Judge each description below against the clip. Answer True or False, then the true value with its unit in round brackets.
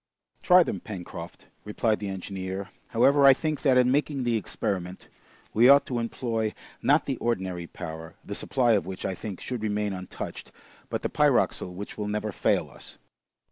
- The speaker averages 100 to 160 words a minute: False (175 wpm)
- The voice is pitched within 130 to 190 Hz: False (105 Hz)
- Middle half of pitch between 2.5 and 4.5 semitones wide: False (5.0 semitones)